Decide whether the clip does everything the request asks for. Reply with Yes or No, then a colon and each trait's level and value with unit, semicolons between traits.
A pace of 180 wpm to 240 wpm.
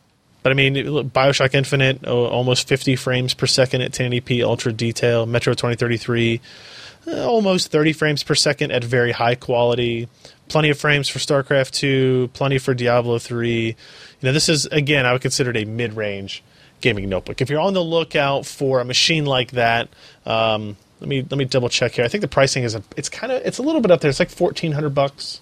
Yes: average, 200 wpm